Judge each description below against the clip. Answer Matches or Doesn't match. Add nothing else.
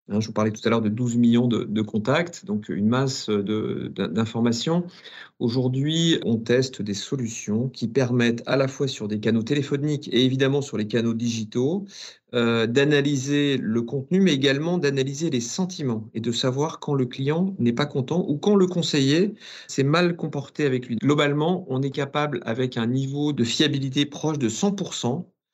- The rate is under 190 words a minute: Matches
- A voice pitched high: Doesn't match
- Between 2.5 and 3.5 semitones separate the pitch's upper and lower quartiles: Doesn't match